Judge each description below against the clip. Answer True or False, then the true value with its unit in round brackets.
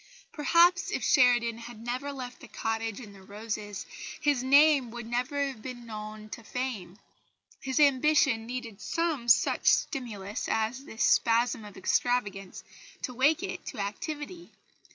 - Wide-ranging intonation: False (4.0 semitones)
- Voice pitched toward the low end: False (245 Hz)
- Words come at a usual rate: True (145 wpm)